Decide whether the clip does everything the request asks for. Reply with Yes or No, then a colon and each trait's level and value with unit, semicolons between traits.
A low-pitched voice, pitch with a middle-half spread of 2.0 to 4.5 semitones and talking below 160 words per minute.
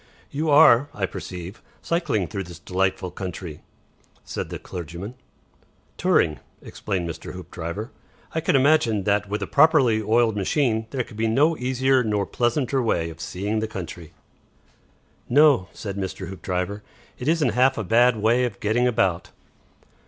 No: low, 110 Hz; average, 5.2 semitones; average, 150 wpm